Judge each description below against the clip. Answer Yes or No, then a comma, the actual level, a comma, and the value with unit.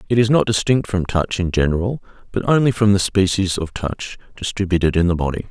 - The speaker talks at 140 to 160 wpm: No, fast, 205 wpm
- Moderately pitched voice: No, very low, 95 Hz